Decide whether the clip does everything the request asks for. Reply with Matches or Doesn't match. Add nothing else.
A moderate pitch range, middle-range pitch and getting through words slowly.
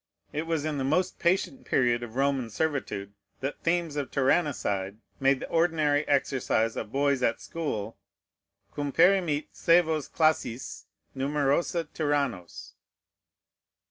Matches